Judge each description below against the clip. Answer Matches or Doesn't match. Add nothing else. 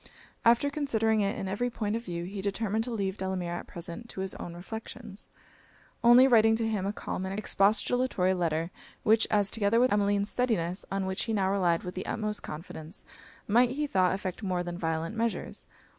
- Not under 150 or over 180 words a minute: Doesn't match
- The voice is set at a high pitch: Matches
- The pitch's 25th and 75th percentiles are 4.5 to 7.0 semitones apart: Doesn't match